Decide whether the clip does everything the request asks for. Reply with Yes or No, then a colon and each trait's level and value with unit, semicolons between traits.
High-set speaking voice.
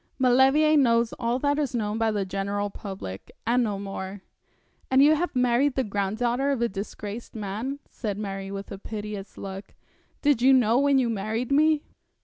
Yes: high, 230 Hz